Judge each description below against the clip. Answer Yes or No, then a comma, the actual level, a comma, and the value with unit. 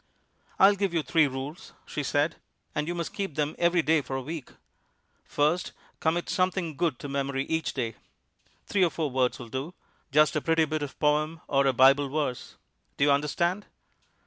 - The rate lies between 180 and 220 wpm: Yes, average, 185 wpm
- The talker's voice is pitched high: No, medium, 150 Hz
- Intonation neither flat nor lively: Yes, average, 3.4 semitones